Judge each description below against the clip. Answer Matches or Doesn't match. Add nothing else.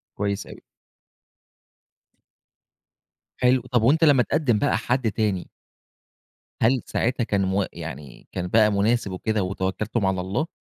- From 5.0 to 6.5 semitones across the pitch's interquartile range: Doesn't match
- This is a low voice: Matches